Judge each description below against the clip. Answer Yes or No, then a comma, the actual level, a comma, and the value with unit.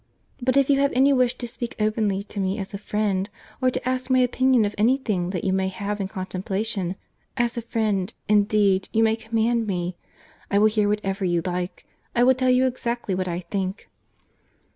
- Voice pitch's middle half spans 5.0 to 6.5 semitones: No, average, 4.0 semitones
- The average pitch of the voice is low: No, high, 210 Hz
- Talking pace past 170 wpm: Yes, average, 195 wpm